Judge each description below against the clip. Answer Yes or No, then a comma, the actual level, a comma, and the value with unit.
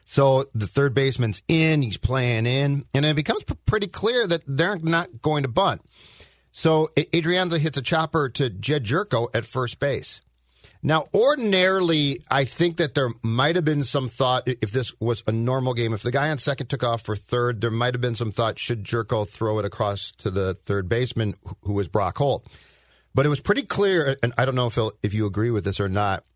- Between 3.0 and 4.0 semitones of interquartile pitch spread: No, wide, 5.5 semitones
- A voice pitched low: Yes, low, 130 Hz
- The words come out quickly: Yes, fast, 210 wpm